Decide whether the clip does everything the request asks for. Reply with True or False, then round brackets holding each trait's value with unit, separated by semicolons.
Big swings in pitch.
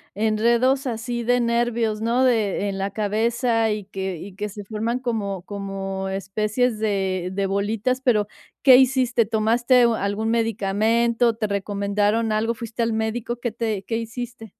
False (2.7 semitones)